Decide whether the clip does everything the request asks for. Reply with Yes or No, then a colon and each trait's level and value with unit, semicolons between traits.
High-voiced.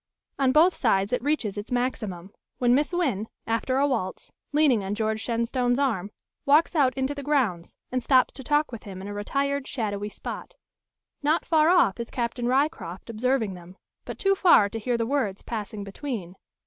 Yes: high, 245 Hz